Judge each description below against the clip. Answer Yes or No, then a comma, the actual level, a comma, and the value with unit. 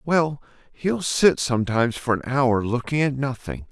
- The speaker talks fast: No, average, 160 wpm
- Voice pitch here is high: No, low, 130 Hz